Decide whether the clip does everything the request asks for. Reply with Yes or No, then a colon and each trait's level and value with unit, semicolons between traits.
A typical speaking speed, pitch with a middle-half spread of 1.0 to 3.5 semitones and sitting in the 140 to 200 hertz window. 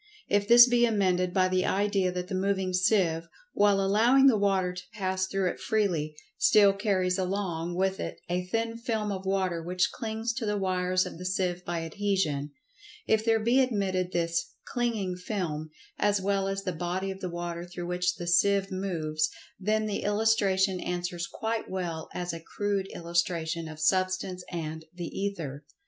Yes: average, 170 wpm; narrow, 2.6 semitones; medium, 185 Hz